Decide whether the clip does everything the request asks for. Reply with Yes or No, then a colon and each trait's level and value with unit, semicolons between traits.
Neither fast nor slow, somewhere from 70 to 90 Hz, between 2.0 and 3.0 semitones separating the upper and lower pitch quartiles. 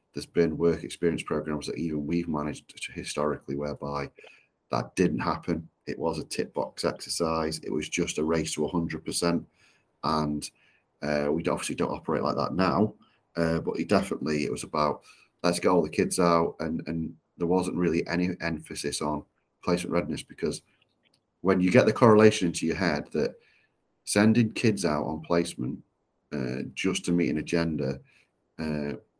Yes: average, 170 wpm; very low, 80 Hz; narrow, 2.5 semitones